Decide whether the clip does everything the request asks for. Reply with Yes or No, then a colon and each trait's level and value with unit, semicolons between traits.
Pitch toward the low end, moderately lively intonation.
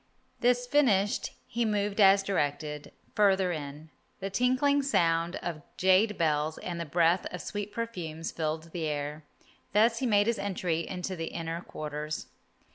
No: medium, 180 Hz; average, 4.6 semitones